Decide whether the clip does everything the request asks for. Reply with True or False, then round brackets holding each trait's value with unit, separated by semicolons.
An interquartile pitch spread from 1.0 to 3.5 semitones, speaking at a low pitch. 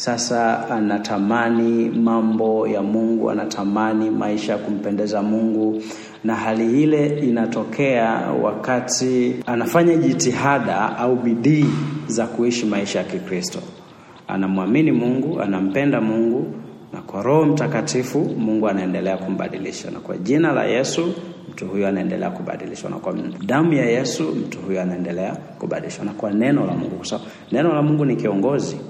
True (3.1 semitones; 115 Hz)